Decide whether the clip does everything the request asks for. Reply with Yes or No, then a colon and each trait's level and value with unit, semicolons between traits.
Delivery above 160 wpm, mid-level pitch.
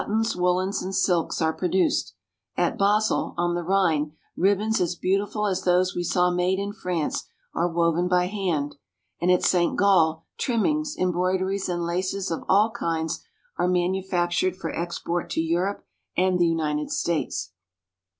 No: average, 155 wpm; medium, 180 Hz